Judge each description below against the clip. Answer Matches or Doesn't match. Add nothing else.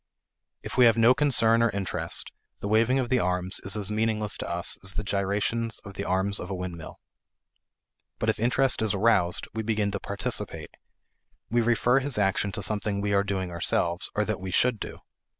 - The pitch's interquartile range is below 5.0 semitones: Matches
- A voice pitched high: Doesn't match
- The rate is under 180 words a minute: Doesn't match